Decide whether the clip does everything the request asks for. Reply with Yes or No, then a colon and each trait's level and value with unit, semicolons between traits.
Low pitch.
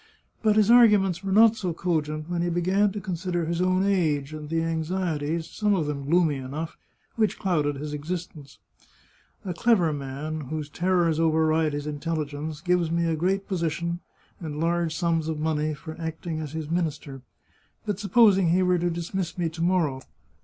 No: medium, 165 Hz